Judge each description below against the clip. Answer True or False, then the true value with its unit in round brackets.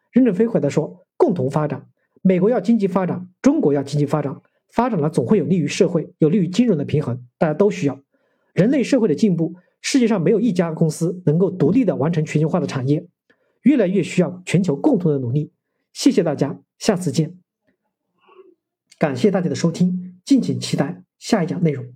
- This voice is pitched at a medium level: True (180 Hz)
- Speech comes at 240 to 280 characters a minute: False (305 characters per minute)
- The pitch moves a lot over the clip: True (6.2 semitones)